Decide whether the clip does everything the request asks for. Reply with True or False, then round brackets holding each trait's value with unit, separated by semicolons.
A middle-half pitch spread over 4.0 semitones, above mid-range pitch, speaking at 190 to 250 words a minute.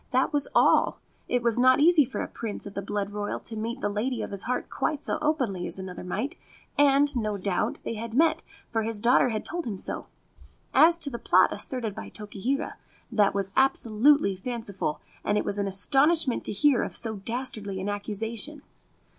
True (4.8 semitones; 230 Hz; 195 wpm)